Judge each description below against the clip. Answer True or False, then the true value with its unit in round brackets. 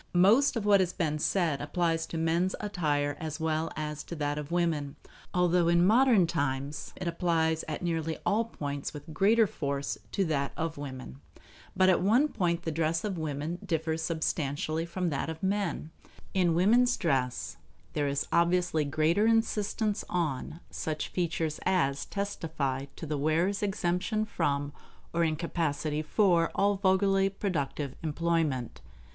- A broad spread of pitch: False (3.8 semitones)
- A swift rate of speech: False (150 wpm)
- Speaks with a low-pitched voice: False (165 Hz)